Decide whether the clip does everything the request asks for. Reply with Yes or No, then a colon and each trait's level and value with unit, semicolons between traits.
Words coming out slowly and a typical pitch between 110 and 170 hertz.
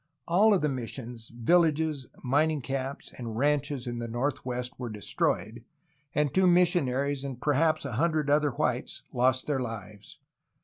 No: average, 150 wpm; low, 135 Hz